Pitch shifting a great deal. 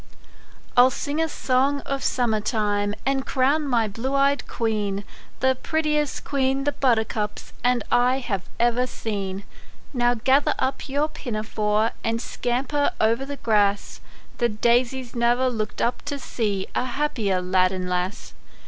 No: average, 4.1 semitones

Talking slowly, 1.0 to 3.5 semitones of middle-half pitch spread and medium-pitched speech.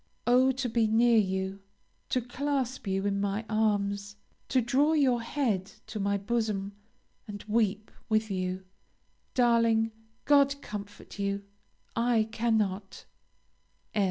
No: slow, 120 wpm; average, 3.2 semitones; high, 220 Hz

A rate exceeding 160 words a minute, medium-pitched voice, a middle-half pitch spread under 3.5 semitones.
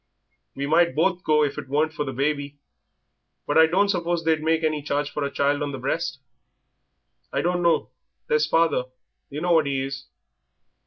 Yes: average, 180 wpm; medium, 150 Hz; narrow, 2.6 semitones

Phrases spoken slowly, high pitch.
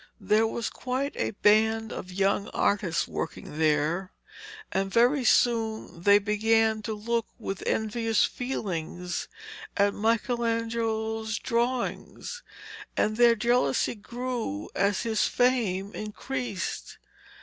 Yes: slow, 105 wpm; high, 220 Hz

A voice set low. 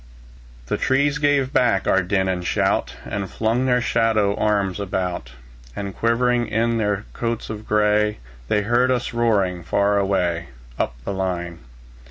Yes: low, 105 Hz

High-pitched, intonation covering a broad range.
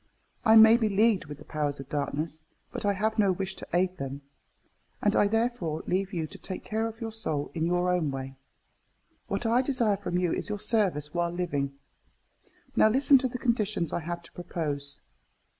No: medium, 180 Hz; wide, 5.8 semitones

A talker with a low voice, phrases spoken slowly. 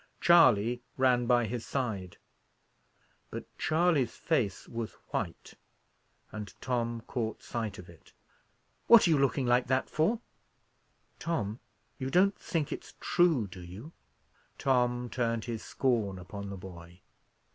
Yes: low, 120 Hz; slow, 130 wpm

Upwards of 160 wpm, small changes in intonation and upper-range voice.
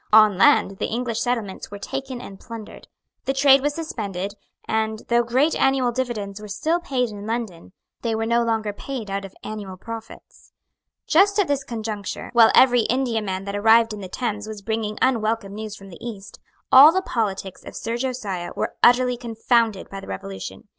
No: average, 180 wpm; average, 3.4 semitones; high, 225 Hz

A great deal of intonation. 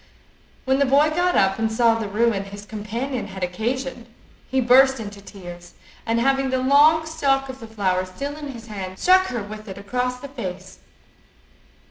No: average, 5.0 semitones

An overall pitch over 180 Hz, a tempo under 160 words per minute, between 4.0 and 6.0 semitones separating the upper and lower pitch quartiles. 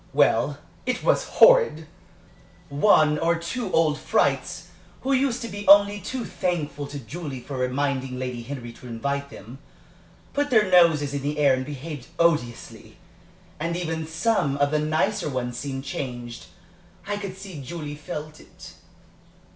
No: medium, 150 Hz; average, 150 wpm; average, 4.9 semitones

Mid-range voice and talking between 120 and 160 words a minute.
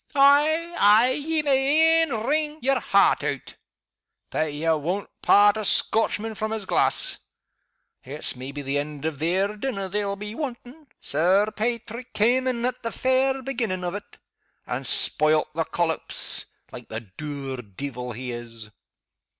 No: high, 205 Hz; average, 150 wpm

